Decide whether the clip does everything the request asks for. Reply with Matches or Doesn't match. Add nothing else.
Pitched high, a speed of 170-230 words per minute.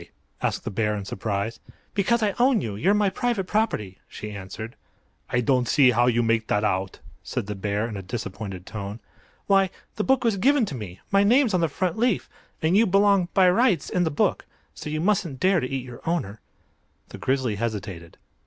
Doesn't match